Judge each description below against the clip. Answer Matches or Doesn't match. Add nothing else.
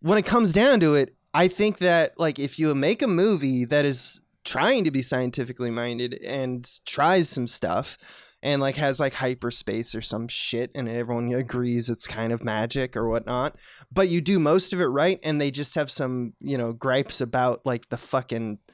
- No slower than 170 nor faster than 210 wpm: Matches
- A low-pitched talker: Matches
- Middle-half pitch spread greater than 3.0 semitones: Matches